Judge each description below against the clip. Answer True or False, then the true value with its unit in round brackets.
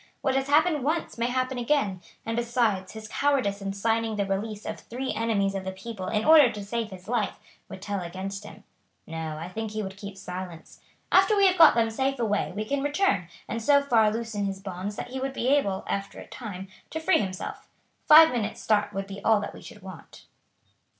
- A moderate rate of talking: False (215 wpm)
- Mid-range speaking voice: False (215 Hz)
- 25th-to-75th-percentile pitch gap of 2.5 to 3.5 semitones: False (4.7 semitones)